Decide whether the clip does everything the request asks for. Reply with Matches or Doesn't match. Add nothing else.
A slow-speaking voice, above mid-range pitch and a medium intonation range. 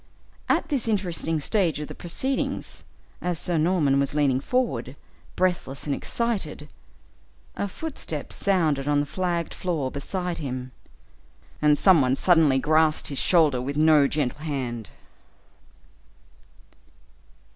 Doesn't match